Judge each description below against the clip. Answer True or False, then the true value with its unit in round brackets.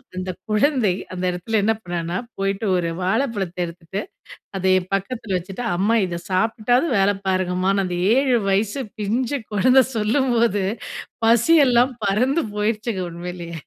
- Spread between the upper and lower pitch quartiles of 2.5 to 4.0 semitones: False (4.4 semitones)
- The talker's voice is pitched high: True (205 Hz)